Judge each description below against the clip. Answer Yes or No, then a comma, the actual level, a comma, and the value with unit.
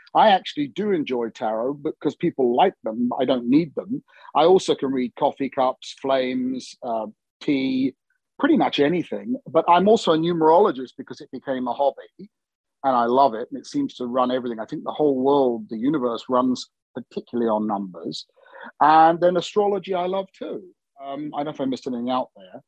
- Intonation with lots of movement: Yes, wide, 7.3 semitones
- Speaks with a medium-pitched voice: Yes, medium, 145 Hz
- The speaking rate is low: No, average, 190 wpm